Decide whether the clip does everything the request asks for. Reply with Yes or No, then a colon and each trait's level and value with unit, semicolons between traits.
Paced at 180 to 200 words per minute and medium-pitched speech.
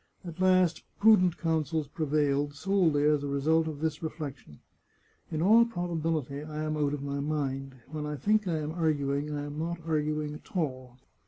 Yes: average, 185 wpm; medium, 155 Hz